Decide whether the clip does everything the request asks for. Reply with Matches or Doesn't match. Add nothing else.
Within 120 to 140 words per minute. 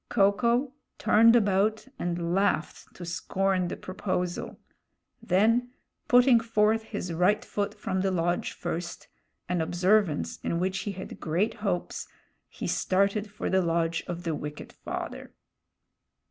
Matches